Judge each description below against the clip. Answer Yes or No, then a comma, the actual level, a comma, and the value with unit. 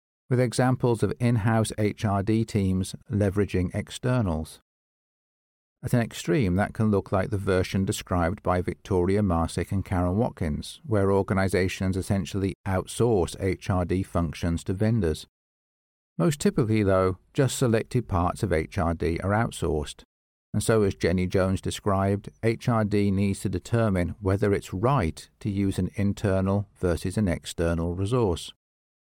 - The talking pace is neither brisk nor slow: No, slow, 130 wpm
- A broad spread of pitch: No, average, 3.3 semitones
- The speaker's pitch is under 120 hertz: Yes, low, 100 Hz